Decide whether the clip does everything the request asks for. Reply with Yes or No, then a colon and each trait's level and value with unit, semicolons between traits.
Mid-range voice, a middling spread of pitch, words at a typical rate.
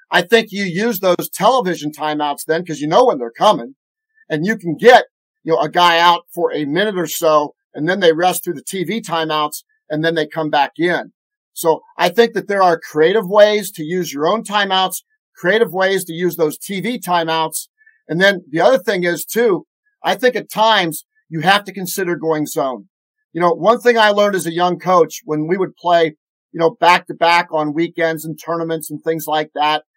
No: medium, 175 Hz; average, 4.5 semitones; fast, 210 wpm